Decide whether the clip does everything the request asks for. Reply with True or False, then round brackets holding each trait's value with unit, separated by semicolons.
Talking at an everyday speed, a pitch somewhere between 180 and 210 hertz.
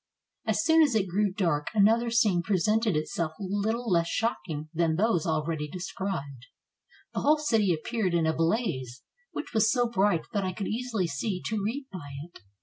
True (175 wpm; 190 Hz)